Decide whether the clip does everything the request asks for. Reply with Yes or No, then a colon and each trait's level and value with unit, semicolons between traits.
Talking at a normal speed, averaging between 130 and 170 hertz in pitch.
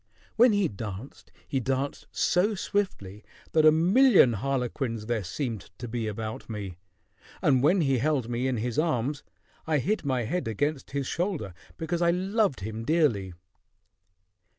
Yes: average, 150 wpm; low, 135 Hz